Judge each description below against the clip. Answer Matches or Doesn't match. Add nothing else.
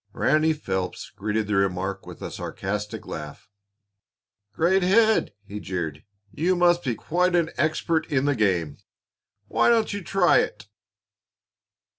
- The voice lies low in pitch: Matches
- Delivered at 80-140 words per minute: Matches